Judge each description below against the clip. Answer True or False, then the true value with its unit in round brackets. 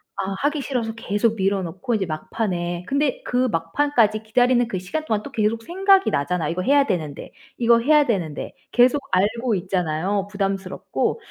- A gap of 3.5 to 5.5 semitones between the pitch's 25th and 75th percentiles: True (5.2 semitones)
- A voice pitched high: True (215 Hz)